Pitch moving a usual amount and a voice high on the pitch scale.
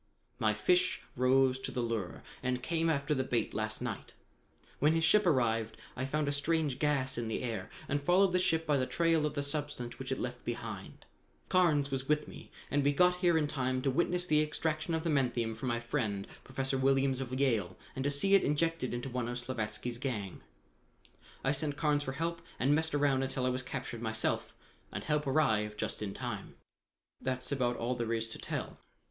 No: average, 3.8 semitones; low, 135 Hz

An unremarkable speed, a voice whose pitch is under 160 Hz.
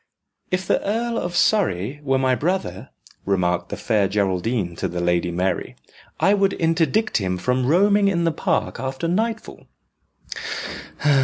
Yes: average, 145 wpm; low, 135 Hz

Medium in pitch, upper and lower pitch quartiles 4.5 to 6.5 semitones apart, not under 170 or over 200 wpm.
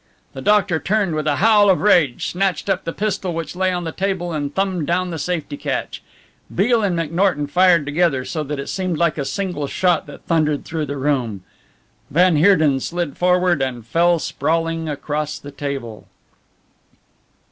No: medium, 165 Hz; average, 3.8 semitones; average, 175 wpm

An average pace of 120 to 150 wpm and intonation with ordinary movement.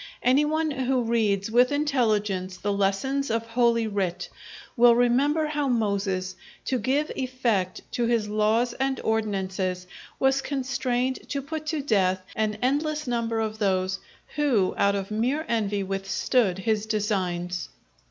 Yes: average, 140 wpm; average, 4.8 semitones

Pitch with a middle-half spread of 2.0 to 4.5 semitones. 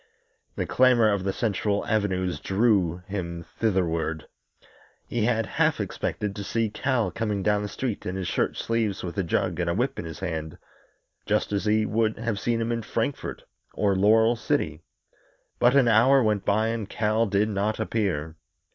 Yes: average, 3.3 semitones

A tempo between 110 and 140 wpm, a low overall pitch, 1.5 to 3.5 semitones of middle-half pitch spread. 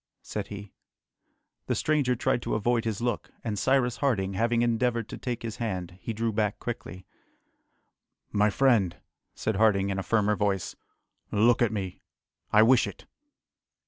No: average, 155 wpm; low, 110 Hz; average, 2.9 semitones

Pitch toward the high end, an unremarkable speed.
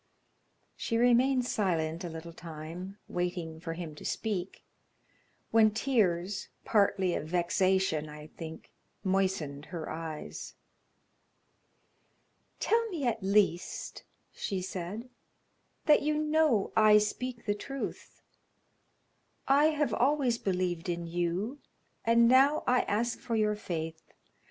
No: high, 195 Hz; slow, 115 wpm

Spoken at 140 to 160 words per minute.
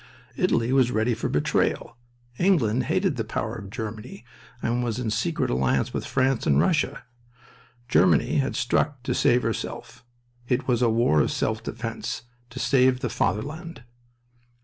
Yes: average, 150 wpm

